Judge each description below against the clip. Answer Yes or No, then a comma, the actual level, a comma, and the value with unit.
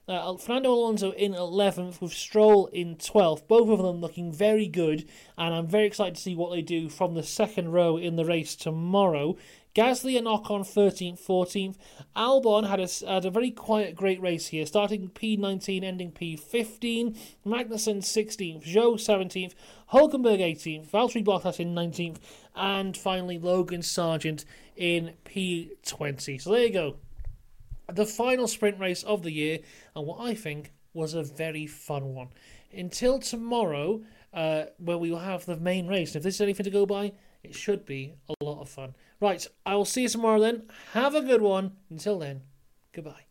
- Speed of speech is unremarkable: Yes, average, 175 wpm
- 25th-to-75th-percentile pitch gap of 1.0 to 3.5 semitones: No, average, 4.2 semitones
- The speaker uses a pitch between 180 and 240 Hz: Yes, medium, 185 Hz